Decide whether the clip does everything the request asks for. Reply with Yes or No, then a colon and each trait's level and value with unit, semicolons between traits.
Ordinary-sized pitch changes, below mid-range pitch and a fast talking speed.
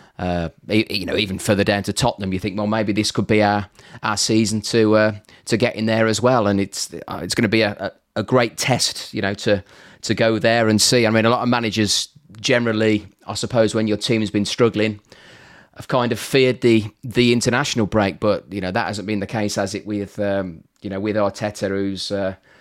No: narrow, 1.9 semitones; low, 105 Hz; fast, 225 wpm